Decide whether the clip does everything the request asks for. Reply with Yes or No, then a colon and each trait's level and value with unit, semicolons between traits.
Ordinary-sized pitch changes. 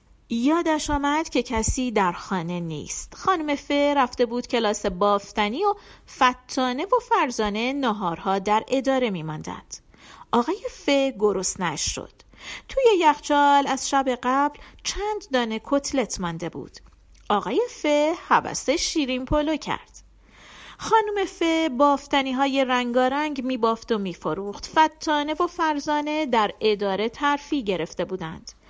No: wide, 5.9 semitones